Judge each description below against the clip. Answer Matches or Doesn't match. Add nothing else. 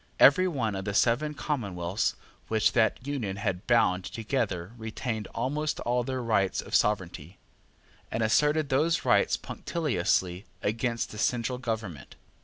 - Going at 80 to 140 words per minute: Matches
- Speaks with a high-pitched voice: Doesn't match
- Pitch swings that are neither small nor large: Matches